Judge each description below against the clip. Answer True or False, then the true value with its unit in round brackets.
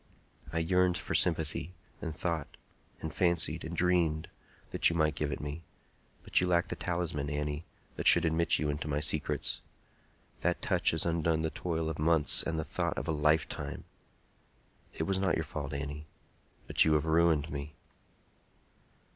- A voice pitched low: True (80 Hz)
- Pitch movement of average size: False (2.0 semitones)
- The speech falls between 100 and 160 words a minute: False (170 wpm)